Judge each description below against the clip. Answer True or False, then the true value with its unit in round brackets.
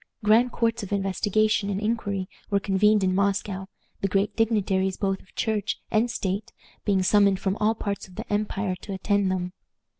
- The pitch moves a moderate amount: False (1.9 semitones)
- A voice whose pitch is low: False (200 Hz)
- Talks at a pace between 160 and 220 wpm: True (175 wpm)